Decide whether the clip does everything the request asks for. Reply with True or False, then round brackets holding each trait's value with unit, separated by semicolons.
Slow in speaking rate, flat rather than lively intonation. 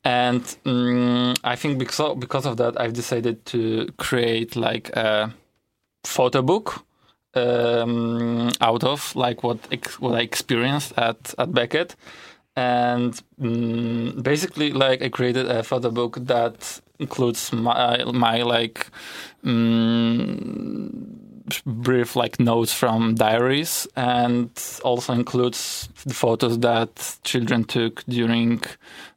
False (120 wpm; 1.4 semitones)